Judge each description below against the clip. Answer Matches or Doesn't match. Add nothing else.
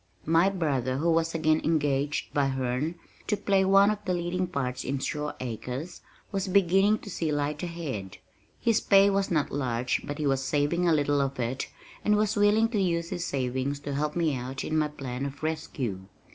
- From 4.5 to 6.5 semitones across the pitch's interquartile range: Matches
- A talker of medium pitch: Matches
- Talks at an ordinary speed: Matches